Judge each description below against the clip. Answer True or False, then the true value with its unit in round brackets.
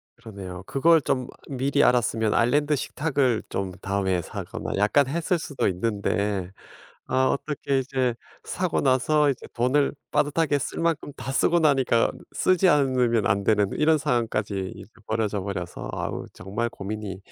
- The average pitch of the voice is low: True (125 Hz)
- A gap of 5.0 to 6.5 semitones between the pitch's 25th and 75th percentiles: True (5.9 semitones)